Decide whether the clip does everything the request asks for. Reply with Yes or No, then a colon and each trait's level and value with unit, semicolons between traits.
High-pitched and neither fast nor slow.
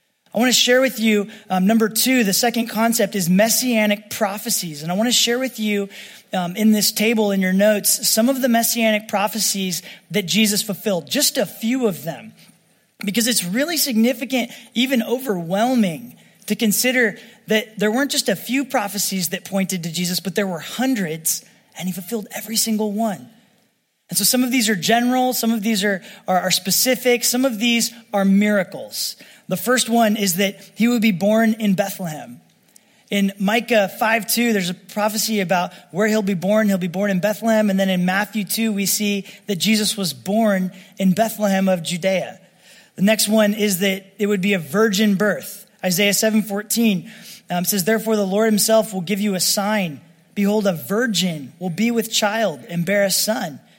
Yes: high, 210 Hz; average, 190 wpm